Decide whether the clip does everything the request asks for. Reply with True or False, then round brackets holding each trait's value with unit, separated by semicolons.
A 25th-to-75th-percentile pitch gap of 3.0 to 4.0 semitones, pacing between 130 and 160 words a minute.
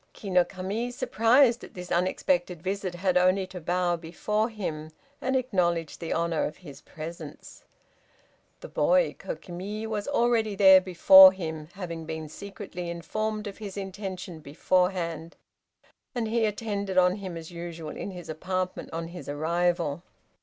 True (3.3 semitones; 145 wpm)